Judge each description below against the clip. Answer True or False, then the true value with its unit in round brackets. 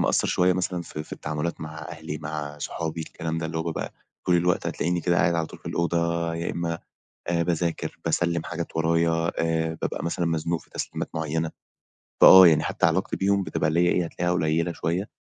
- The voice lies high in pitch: False (85 Hz)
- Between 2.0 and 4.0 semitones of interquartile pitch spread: False (1.2 semitones)